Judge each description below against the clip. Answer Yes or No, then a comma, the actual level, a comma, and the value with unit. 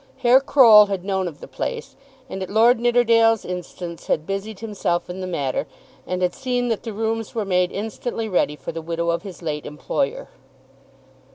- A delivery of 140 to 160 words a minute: No, average, 185 wpm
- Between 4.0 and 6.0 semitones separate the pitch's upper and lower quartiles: Yes, average, 4.4 semitones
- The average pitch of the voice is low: No, high, 200 Hz